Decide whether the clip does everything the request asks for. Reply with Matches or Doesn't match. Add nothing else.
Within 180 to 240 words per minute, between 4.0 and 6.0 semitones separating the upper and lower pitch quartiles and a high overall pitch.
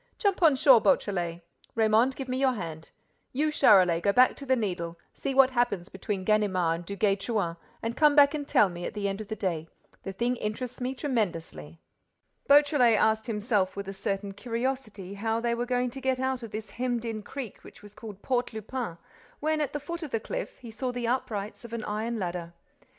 Matches